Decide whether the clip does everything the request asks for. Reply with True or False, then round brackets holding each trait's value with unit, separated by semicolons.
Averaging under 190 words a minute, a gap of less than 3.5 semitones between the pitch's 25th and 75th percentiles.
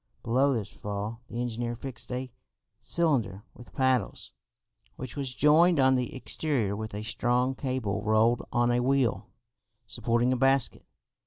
True (145 wpm; 3.0 semitones)